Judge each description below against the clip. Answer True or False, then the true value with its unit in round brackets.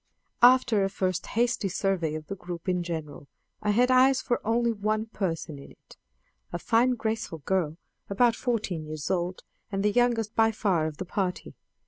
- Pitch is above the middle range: True (200 Hz)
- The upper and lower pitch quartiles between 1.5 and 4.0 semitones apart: False (4.8 semitones)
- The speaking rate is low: False (175 wpm)